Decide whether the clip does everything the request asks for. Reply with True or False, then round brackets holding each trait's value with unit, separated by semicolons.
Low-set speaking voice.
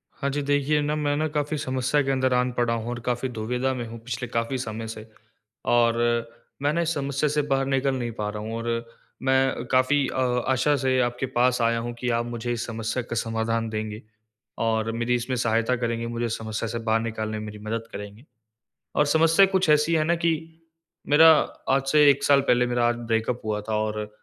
True (120 Hz)